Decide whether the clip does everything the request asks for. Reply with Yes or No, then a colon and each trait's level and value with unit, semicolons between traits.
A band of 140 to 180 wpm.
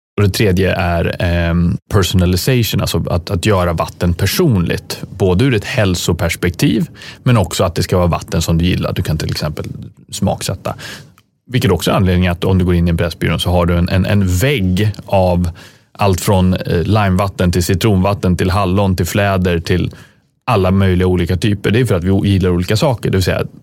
No: average, 190 wpm